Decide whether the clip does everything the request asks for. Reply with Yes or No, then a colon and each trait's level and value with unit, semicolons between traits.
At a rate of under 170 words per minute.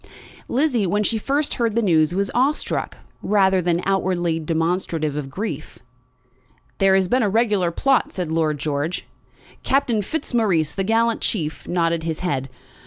Yes: average, 155 wpm